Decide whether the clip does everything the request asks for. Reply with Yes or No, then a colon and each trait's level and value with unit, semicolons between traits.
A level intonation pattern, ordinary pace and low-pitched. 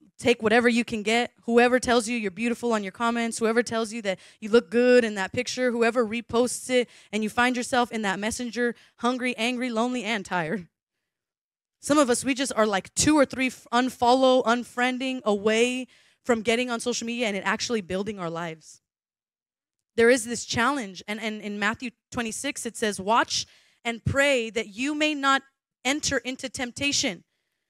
No: narrow, 2.3 semitones; average, 180 wpm; high, 235 Hz